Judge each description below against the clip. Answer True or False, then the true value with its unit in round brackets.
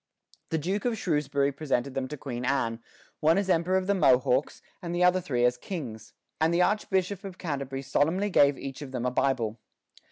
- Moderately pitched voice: True (145 Hz)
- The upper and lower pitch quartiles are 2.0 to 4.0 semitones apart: False (5.6 semitones)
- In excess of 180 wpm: True (195 wpm)